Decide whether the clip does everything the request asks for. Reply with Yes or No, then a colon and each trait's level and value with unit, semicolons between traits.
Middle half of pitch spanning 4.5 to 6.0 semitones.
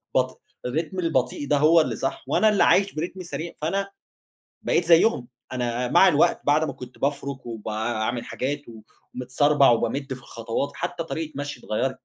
Yes: average, 4.8 semitones